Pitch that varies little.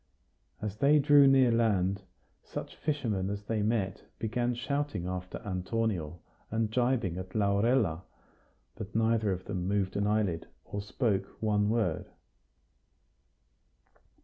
No: average, 3.6 semitones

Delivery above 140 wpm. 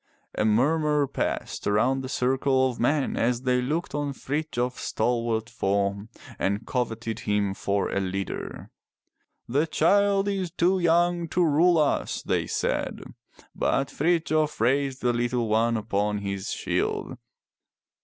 No: slow, 135 wpm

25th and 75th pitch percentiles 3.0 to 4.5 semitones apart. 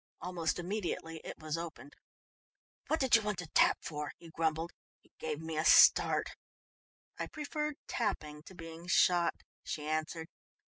No: narrow, 2.6 semitones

